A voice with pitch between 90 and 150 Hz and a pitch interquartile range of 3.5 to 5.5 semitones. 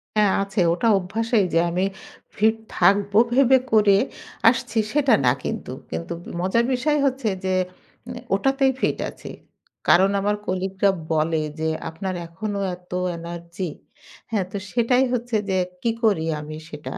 No: high, 200 Hz; average, 4.5 semitones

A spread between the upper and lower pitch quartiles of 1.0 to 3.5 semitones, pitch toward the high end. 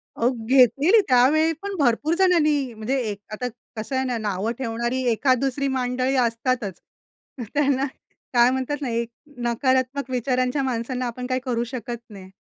Yes: narrow, 2.6 semitones; very high, 255 Hz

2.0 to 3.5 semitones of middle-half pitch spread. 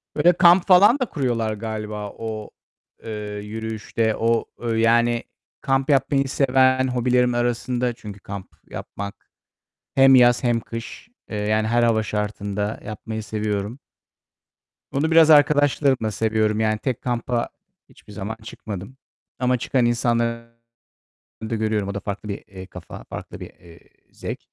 Yes: average, 3.1 semitones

